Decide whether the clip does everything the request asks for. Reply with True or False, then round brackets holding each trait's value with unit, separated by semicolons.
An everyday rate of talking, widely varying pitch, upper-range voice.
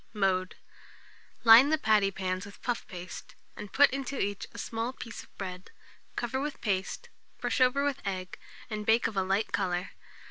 False (175 wpm; 4.8 semitones; 210 Hz)